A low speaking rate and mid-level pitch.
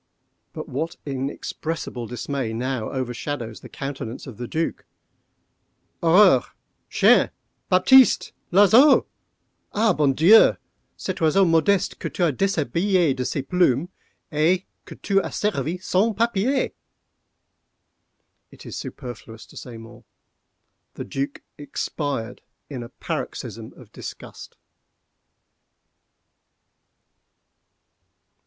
Yes: slow, 95 wpm; medium, 155 Hz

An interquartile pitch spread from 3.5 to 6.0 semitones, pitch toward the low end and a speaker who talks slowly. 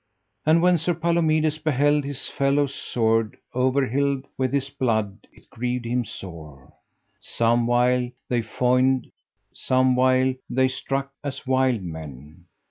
No: average, 3.1 semitones; low, 130 Hz; slow, 130 wpm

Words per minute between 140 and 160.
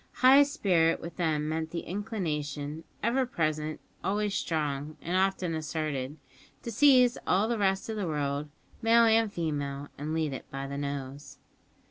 Yes: average, 155 wpm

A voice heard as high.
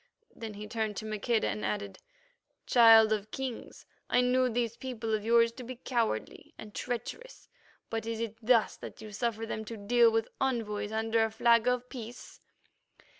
Yes: high, 225 Hz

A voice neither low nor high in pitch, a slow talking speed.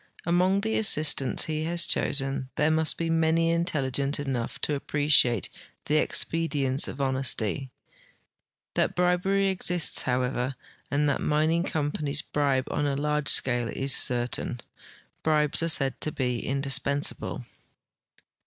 Yes: medium, 145 Hz; slow, 125 wpm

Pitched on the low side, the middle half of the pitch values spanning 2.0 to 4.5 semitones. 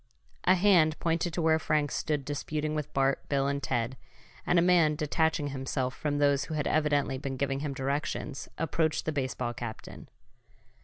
No: medium, 145 Hz; narrow, 2.5 semitones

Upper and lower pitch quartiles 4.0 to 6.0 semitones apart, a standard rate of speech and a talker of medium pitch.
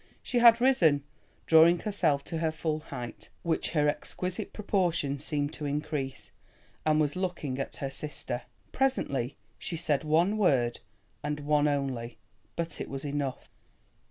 No: average, 3.4 semitones; average, 145 wpm; medium, 150 Hz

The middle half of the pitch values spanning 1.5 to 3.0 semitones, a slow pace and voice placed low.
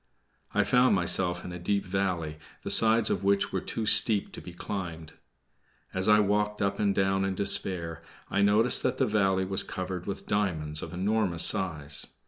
No: average, 2.7 semitones; average, 180 wpm; very low, 95 Hz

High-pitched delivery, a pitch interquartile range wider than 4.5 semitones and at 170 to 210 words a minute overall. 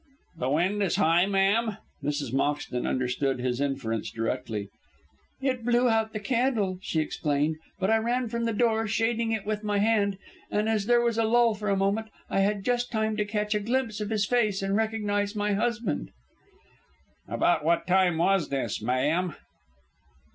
Yes: high, 205 Hz; average, 5.3 semitones; average, 175 wpm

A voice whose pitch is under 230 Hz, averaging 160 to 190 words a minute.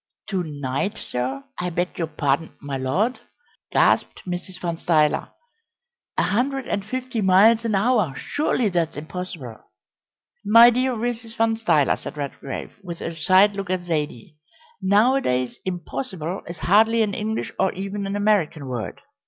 No: medium, 185 Hz; average, 145 wpm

